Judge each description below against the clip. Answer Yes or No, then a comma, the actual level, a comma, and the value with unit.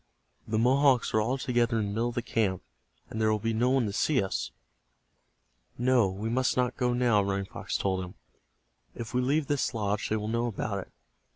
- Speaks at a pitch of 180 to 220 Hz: No, low, 115 Hz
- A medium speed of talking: No, fast, 210 wpm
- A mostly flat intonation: No, average, 3.1 semitones